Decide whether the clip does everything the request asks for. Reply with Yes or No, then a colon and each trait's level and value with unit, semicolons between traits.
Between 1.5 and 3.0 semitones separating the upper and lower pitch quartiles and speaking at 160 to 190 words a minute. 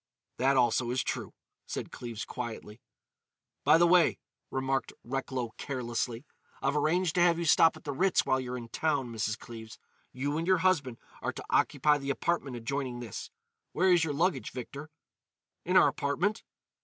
No: average, 4.9 semitones; average, 170 wpm